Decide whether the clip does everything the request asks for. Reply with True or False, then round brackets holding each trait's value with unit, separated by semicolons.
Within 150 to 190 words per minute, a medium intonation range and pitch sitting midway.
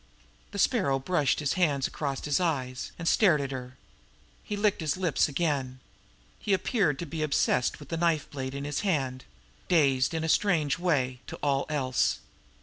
True (175 wpm; 4.2 semitones; 145 Hz)